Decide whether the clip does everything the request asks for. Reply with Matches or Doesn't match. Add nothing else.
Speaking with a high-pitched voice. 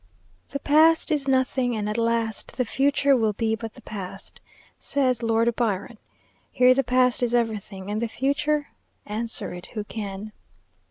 Matches